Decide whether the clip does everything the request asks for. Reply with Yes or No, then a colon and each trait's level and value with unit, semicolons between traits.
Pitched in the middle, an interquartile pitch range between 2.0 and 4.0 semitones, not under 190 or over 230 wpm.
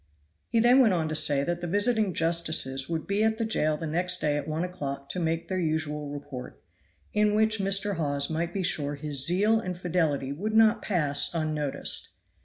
No: medium, 165 Hz; average, 5.0 semitones; average, 200 wpm